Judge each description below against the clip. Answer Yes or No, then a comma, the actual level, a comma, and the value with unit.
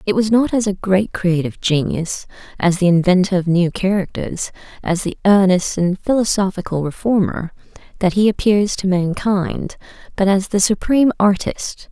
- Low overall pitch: No, high, 190 Hz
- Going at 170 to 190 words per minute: No, average, 150 wpm